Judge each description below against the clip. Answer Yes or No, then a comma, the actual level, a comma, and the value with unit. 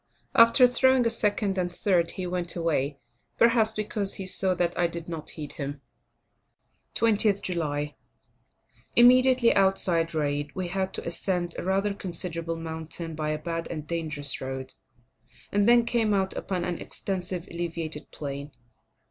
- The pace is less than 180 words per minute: Yes, average, 150 wpm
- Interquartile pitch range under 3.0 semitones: No, average, 3.8 semitones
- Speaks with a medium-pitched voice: Yes, medium, 175 Hz